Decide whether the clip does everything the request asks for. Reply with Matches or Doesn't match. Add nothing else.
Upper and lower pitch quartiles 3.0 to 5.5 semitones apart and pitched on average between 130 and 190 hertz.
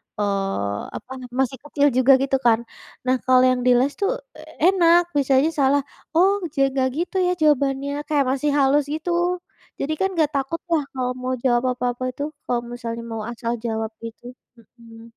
Doesn't match